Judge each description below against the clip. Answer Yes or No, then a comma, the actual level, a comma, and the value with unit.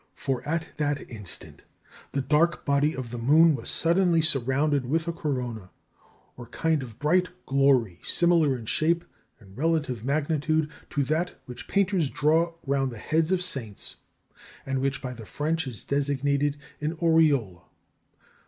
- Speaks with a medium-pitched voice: Yes, medium, 145 Hz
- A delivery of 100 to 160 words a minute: Yes, average, 150 wpm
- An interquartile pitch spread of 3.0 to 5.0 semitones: Yes, average, 3.9 semitones